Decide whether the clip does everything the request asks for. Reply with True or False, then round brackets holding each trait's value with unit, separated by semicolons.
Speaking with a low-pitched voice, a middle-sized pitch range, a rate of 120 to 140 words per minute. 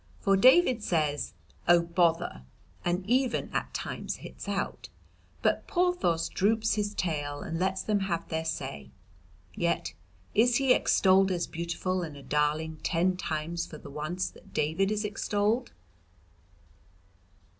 False (180 Hz; 4.5 semitones; 135 wpm)